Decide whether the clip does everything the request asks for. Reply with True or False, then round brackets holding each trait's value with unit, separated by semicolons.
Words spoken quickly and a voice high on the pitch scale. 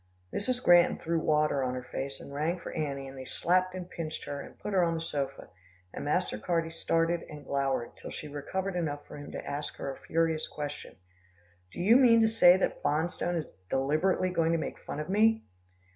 False (210 wpm; 165 Hz)